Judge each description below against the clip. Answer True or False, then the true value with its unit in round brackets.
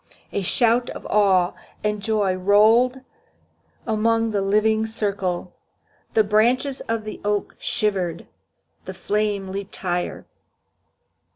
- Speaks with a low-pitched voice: False (210 Hz)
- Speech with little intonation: True (2.2 semitones)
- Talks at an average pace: False (110 wpm)